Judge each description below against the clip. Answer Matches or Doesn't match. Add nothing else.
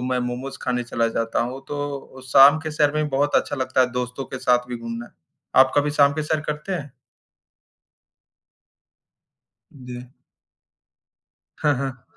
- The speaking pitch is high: Doesn't match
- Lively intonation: Doesn't match